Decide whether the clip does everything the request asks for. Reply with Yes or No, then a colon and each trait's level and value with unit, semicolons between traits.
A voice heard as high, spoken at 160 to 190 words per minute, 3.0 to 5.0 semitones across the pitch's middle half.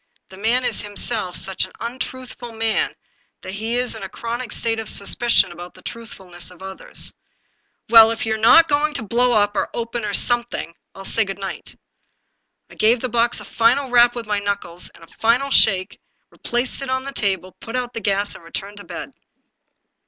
No: high, 225 Hz; fast, 205 wpm; average, 3.4 semitones